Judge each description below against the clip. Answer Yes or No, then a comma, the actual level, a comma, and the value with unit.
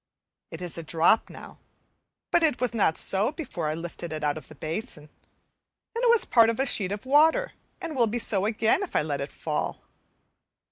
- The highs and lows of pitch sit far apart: Yes, wide, 8.8 semitones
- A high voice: Yes, high, 210 Hz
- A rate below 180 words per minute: No, fast, 205 wpm